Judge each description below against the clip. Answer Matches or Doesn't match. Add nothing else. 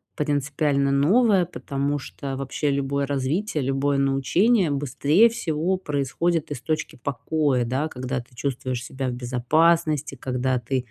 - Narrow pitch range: Doesn't match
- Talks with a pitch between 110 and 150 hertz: Matches